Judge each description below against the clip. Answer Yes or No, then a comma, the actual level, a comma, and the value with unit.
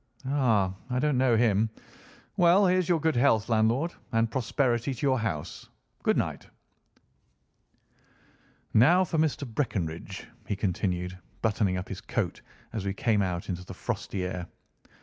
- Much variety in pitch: Yes, wide, 6.3 semitones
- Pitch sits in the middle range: No, low, 115 Hz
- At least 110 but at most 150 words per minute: Yes, average, 145 wpm